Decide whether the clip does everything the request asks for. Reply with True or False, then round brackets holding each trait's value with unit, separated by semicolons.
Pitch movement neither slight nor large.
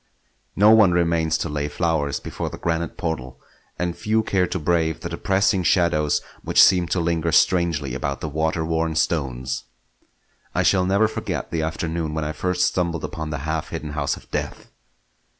False (2.3 semitones)